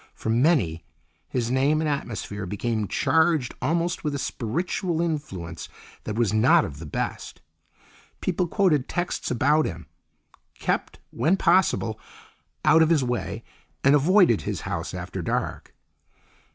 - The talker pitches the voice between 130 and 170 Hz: Yes, medium, 140 Hz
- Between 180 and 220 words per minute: No, slow, 135 wpm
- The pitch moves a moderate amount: No, wide, 6.8 semitones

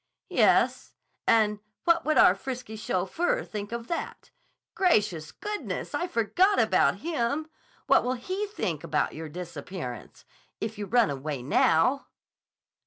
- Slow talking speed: Yes, slow, 130 wpm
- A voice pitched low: No, high, 225 Hz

